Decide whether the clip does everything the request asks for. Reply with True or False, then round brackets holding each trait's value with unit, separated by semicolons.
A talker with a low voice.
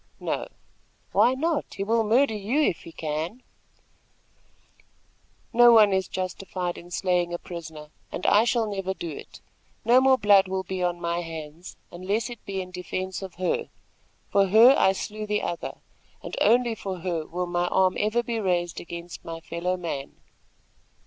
False (190 Hz)